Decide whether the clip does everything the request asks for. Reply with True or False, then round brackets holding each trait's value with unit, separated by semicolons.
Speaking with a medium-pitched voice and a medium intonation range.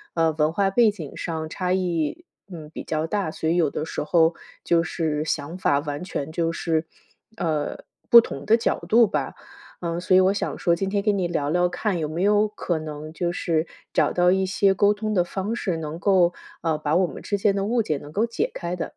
True (175 Hz; 3.7 semitones)